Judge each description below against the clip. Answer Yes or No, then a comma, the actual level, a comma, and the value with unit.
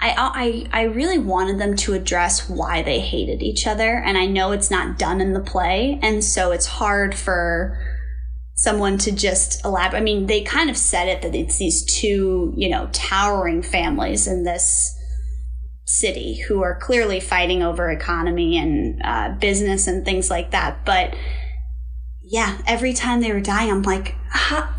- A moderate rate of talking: Yes, average, 175 wpm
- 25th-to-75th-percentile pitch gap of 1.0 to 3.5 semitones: No, average, 4.0 semitones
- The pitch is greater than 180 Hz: Yes, high, 190 Hz